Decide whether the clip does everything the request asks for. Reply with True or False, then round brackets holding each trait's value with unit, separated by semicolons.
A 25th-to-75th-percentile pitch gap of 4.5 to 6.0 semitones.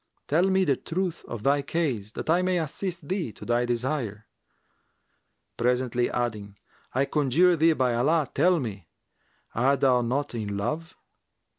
True (5.5 semitones)